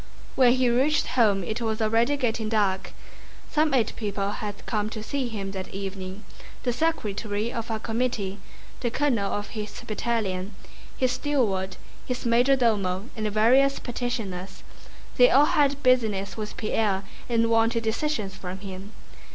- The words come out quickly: No, average, 150 wpm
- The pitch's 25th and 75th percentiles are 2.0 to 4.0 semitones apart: Yes, average, 3.6 semitones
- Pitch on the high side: Yes, high, 220 Hz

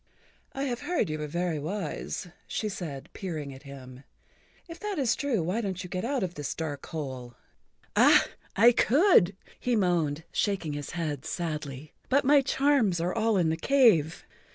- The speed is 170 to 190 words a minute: Yes, average, 175 wpm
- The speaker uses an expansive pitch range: Yes, wide, 7.4 semitones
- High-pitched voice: No, medium, 175 Hz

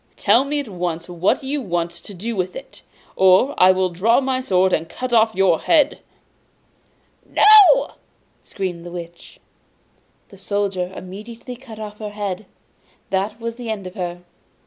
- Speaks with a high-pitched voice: Yes, high, 200 Hz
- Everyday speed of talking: Yes, average, 160 wpm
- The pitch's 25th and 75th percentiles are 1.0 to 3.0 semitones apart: No, average, 4.5 semitones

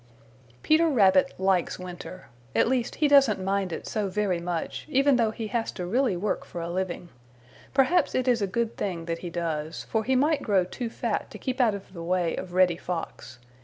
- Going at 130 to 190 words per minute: No, fast, 205 wpm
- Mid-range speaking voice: No, high, 195 Hz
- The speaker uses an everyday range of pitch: No, wide, 5.7 semitones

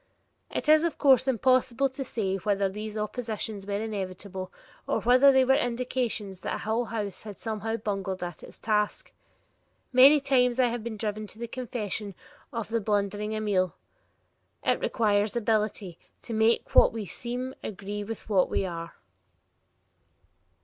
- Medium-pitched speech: No, high, 220 Hz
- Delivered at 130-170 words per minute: Yes, average, 150 wpm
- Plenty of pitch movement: No, average, 3.3 semitones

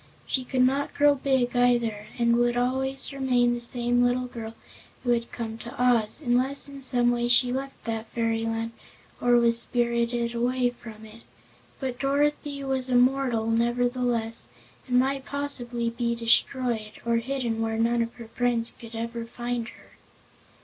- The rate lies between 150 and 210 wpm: Yes, average, 160 wpm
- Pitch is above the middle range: Yes, high, 240 Hz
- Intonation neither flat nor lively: No, narrow, 1.7 semitones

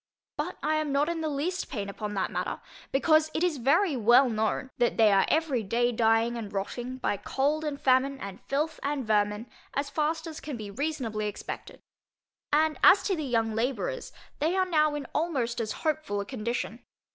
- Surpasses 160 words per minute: Yes, average, 190 wpm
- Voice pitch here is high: Yes, very high, 270 Hz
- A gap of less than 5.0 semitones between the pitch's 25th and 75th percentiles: No, wide, 5.6 semitones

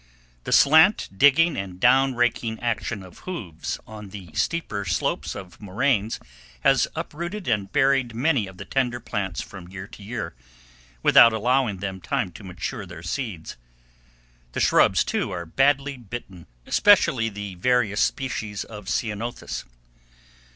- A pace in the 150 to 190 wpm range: No, average, 140 wpm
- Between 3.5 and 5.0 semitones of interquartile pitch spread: No, wide, 5.5 semitones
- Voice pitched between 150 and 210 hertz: No, low, 110 Hz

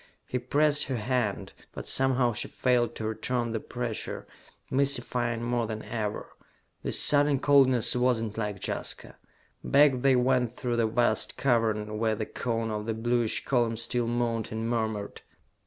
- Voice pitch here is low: Yes, low, 120 Hz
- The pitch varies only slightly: Yes, narrow, 2.2 semitones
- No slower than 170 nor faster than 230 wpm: No, average, 155 wpm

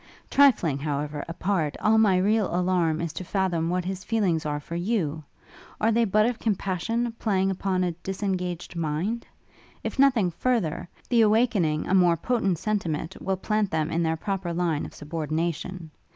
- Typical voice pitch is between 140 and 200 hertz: Yes, medium, 185 Hz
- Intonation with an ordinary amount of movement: Yes, average, 4.5 semitones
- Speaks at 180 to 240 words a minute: No, average, 165 wpm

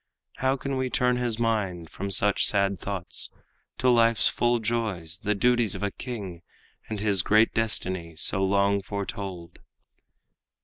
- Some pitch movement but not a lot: Yes, average, 3.5 semitones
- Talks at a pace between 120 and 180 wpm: Yes, average, 145 wpm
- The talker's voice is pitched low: Yes, low, 100 Hz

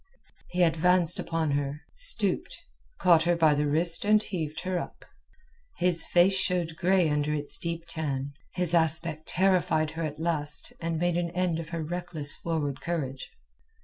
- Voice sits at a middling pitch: Yes, medium, 165 Hz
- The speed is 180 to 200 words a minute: No, average, 160 wpm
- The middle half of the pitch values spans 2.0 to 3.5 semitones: Yes, narrow, 2.4 semitones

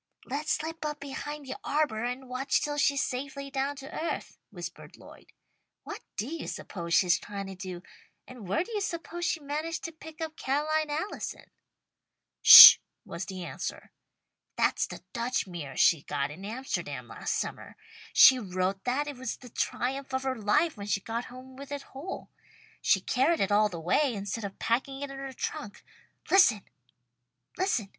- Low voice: No, very high, 260 Hz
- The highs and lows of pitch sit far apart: Yes, wide, 6.3 semitones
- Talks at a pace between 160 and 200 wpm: Yes, average, 175 wpm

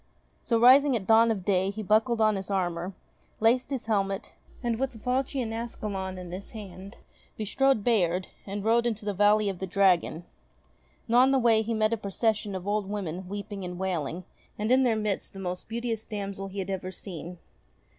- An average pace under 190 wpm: No, average, 195 wpm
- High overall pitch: Yes, high, 205 Hz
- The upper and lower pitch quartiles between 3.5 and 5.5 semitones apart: No, average, 3.1 semitones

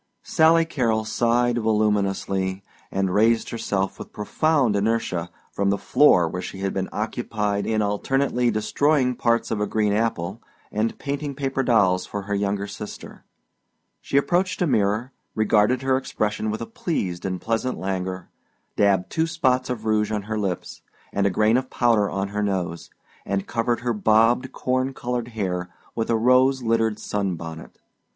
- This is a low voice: Yes, low, 110 Hz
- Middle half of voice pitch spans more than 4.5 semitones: No, average, 3.7 semitones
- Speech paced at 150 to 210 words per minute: Yes, average, 160 wpm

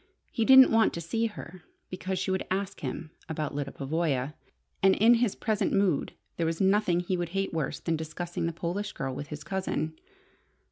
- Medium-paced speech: Yes, average, 190 wpm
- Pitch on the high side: No, medium, 175 Hz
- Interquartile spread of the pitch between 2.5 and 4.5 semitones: Yes, average, 3.7 semitones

